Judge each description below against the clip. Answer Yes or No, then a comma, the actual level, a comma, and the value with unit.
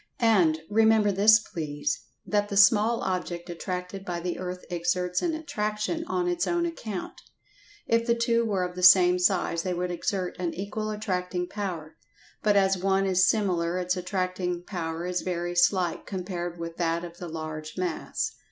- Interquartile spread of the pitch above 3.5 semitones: No, average, 3.1 semitones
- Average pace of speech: Yes, average, 170 wpm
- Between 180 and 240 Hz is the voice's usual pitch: Yes, medium, 185 Hz